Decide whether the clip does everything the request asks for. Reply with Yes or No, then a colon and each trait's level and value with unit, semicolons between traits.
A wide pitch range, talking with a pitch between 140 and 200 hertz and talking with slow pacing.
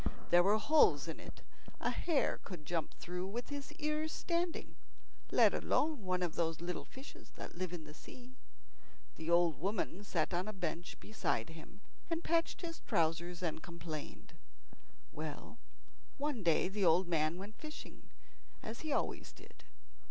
No: wide, 7.6 semitones; medium, 185 Hz; average, 160 wpm